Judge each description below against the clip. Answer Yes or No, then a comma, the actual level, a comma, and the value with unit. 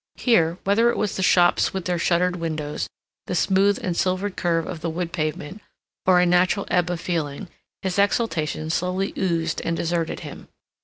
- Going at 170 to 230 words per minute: Yes, average, 175 wpm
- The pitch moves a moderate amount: No, narrow, 2.3 semitones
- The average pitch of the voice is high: No, medium, 180 Hz